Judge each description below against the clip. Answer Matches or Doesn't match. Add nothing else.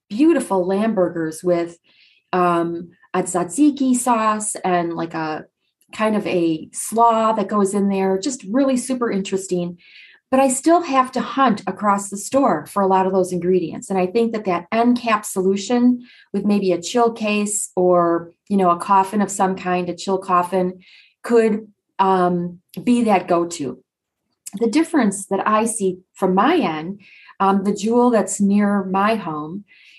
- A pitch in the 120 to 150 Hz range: Doesn't match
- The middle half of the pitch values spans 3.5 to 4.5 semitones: Matches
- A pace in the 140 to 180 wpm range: Matches